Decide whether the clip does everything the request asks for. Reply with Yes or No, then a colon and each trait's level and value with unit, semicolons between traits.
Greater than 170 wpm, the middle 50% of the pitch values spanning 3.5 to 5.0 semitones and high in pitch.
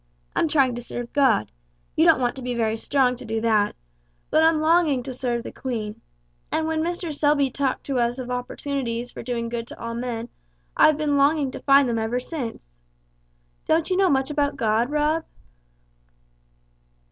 Yes: average, 180 wpm; average, 3.9 semitones; very high, 255 Hz